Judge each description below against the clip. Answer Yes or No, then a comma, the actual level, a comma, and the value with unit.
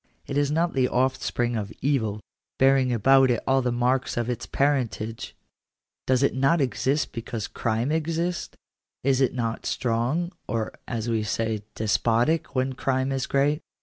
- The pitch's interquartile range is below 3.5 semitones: Yes, average, 2.9 semitones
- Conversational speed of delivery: Yes, average, 155 wpm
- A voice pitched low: Yes, low, 130 Hz